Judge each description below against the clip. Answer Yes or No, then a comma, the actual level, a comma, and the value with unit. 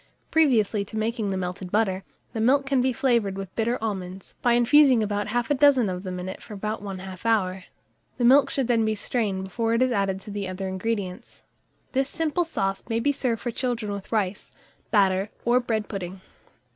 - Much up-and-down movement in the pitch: No, average, 4.0 semitones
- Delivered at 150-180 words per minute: No, average, 200 wpm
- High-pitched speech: Yes, high, 215 Hz